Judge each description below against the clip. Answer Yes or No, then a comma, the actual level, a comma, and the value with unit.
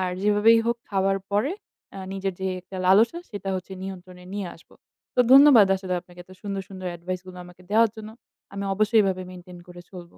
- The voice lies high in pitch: Yes, high, 195 Hz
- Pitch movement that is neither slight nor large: No, narrow, 2.3 semitones